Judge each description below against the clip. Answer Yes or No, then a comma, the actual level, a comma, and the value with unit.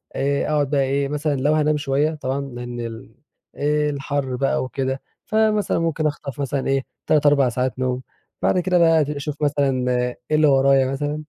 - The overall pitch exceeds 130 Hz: Yes, medium, 140 Hz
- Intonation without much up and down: Yes, narrow, 2.2 semitones